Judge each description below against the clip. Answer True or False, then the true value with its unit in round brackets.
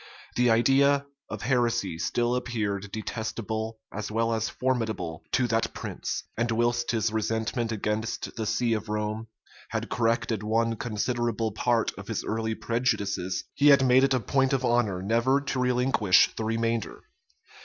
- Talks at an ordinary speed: True (155 wpm)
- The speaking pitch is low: True (115 Hz)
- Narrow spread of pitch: True (2.0 semitones)